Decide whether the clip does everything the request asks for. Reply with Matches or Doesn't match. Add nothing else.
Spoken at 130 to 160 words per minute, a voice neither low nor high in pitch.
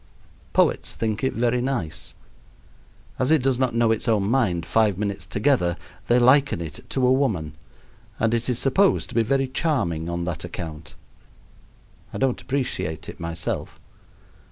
Doesn't match